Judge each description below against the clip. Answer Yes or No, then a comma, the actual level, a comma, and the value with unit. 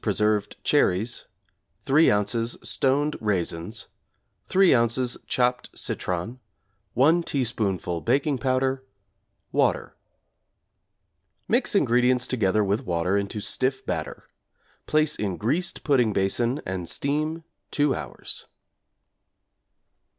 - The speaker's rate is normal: No, slow, 95 wpm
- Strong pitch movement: No, average, 4.9 semitones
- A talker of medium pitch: No, low, 120 Hz